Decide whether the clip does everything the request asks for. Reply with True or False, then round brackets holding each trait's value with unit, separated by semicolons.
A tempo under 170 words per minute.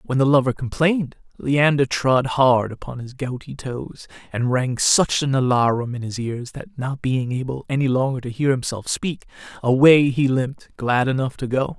False (185 wpm)